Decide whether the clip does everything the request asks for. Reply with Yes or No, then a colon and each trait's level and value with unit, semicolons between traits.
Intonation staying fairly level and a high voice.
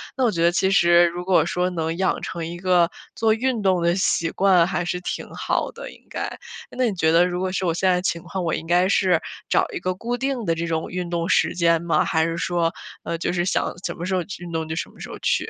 No: narrow, 2.0 semitones; medium, 175 Hz